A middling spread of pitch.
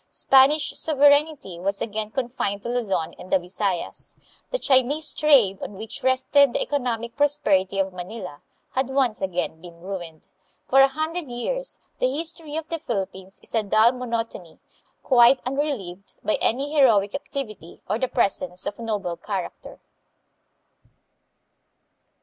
No: wide, 6.1 semitones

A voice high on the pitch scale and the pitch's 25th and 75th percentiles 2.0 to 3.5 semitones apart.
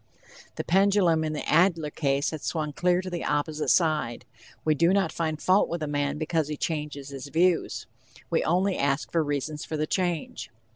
No: medium, 155 Hz; average, 2.8 semitones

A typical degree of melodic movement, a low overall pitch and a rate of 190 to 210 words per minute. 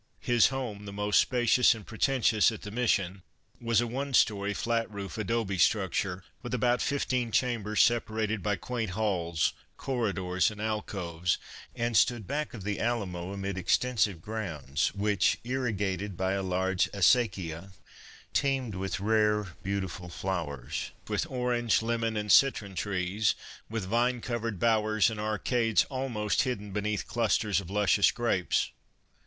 No: average, 3.5 semitones; low, 105 Hz; average, 145 wpm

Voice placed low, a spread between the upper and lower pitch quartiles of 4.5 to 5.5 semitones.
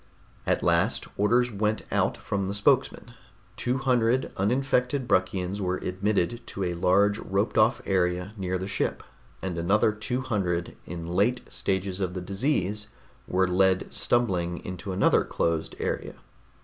No: low, 100 Hz; average, 3.2 semitones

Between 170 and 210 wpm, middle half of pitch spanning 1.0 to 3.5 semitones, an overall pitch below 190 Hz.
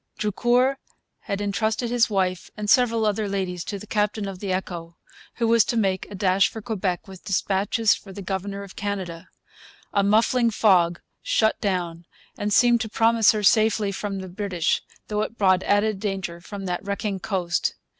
No: average, 175 wpm; narrow, 2.5 semitones; high, 200 Hz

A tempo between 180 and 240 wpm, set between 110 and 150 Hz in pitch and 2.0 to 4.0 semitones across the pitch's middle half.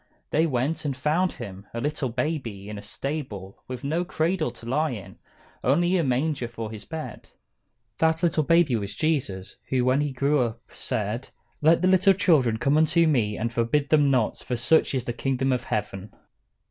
No: average, 190 wpm; low, 135 Hz; average, 5.3 semitones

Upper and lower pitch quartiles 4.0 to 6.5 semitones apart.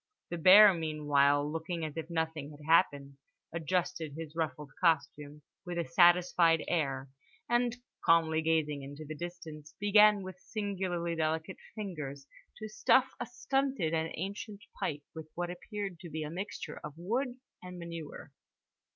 No: average, 3.5 semitones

